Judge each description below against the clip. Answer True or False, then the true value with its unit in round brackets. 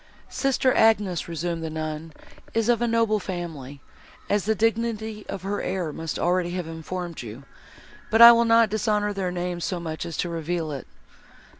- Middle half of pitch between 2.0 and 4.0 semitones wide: False (5.0 semitones)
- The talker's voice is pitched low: False (180 Hz)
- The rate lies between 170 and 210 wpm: True (175 wpm)